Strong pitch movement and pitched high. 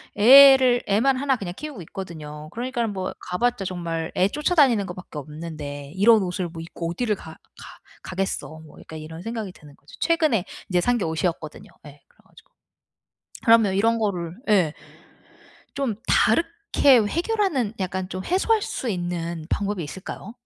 Yes: wide, 6.4 semitones; high, 195 Hz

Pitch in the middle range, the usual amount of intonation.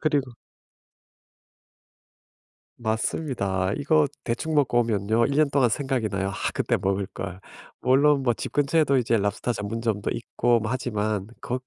No: low, 120 Hz; average, 5.0 semitones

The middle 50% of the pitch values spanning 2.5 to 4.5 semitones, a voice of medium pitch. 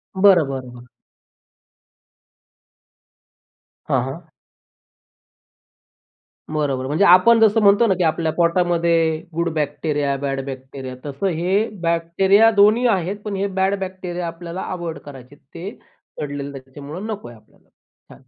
No: average, 5.2 semitones; medium, 170 Hz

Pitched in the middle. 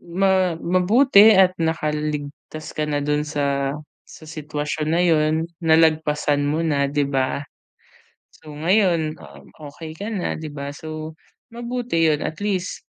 Yes: medium, 155 Hz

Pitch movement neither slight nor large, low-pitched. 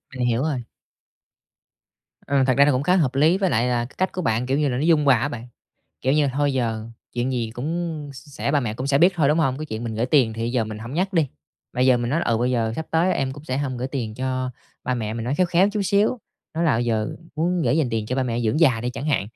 Yes: average, 4.4 semitones; low, 130 Hz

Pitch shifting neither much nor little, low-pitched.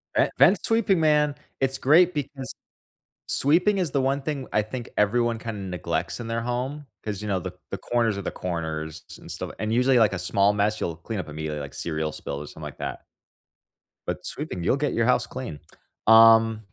No: wide, 6.3 semitones; low, 115 Hz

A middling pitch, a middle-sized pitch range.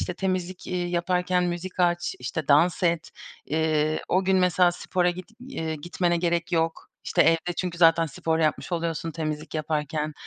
No: medium, 170 Hz; narrow, 2.0 semitones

